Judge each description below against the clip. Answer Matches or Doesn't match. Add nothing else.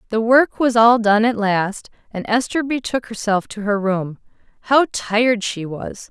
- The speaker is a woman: Matches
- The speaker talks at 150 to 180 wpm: Matches